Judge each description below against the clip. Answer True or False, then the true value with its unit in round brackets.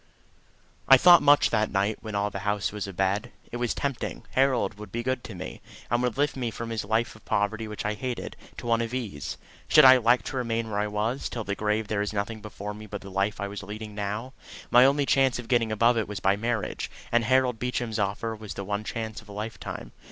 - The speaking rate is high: True (240 wpm)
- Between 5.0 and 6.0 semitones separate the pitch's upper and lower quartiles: False (2.8 semitones)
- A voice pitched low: True (110 Hz)